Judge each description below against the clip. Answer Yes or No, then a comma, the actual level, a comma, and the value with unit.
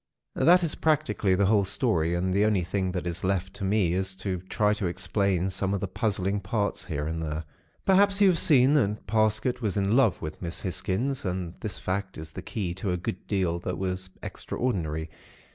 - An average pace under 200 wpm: No, fast, 205 wpm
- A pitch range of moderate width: Yes, average, 3.1 semitones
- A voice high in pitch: No, very low, 95 Hz